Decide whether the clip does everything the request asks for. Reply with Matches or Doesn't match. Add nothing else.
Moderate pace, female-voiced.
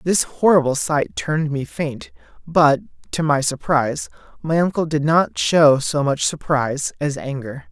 Doesn't match